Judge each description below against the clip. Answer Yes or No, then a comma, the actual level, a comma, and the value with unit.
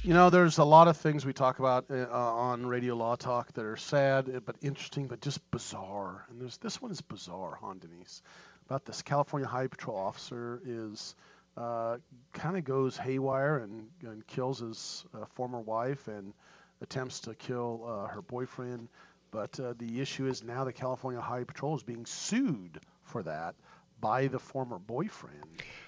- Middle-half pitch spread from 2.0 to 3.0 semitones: Yes, average, 2.7 semitones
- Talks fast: No, average, 180 wpm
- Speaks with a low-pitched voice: Yes, low, 125 Hz